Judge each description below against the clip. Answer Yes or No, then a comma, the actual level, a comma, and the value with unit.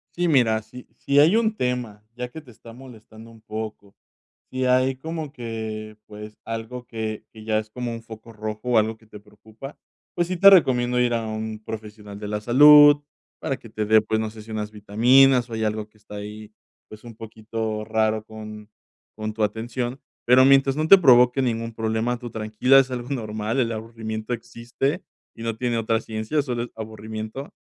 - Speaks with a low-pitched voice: Yes, low, 115 Hz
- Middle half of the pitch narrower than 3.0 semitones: Yes, narrow, 2.6 semitones